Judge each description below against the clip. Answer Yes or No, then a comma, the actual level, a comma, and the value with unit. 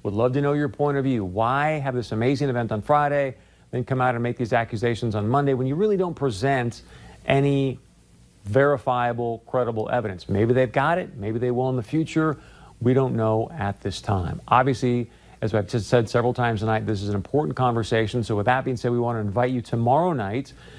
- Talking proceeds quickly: Yes, fast, 215 wpm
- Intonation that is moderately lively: Yes, average, 3.2 semitones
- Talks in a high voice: No, low, 125 Hz